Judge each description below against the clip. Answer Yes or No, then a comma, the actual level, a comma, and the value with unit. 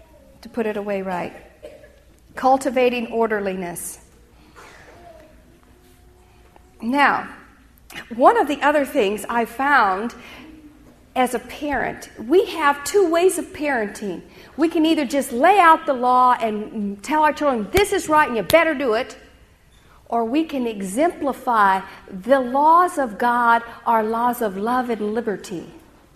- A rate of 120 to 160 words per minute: Yes, slow, 135 wpm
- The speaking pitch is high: Yes, very high, 250 Hz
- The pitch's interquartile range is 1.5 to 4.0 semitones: No, average, 5.2 semitones